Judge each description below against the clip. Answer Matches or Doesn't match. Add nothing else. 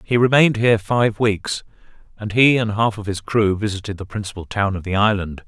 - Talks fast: Matches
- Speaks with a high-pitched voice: Doesn't match